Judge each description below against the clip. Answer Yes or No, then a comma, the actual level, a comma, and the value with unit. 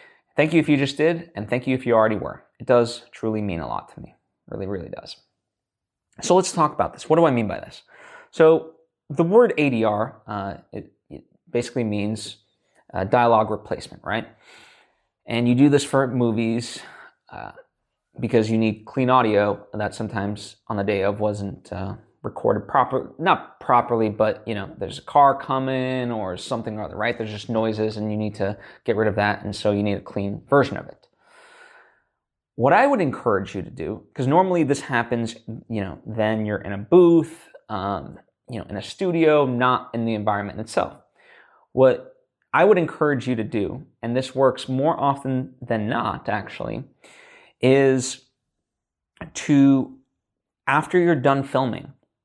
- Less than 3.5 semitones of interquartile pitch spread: No, average, 4.6 semitones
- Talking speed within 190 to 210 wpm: No, average, 180 wpm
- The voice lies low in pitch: Yes, low, 120 Hz